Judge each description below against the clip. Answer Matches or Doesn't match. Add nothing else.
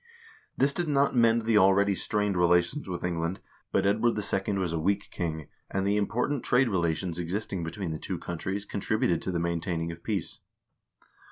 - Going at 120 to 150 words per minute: Doesn't match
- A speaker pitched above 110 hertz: Doesn't match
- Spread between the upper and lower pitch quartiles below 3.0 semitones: Doesn't match